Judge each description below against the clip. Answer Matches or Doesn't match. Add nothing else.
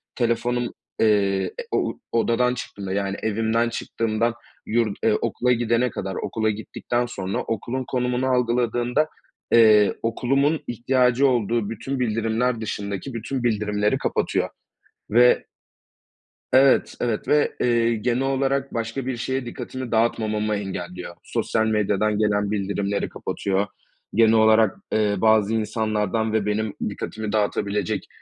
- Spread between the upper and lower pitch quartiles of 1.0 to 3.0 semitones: Matches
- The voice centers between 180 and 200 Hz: Doesn't match